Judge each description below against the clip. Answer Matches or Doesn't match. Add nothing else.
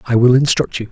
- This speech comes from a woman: Doesn't match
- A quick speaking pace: Matches